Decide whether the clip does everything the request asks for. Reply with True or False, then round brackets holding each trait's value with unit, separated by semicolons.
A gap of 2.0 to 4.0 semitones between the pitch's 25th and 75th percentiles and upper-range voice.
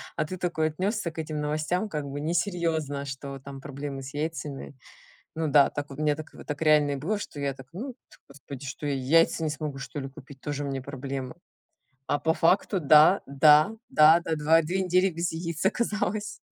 False (3.0 semitones; 150 Hz)